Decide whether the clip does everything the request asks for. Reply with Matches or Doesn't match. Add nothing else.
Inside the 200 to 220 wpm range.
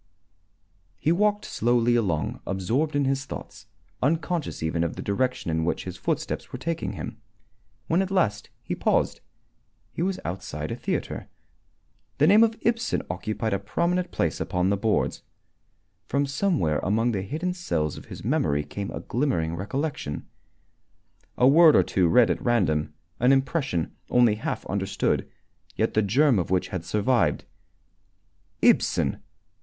Doesn't match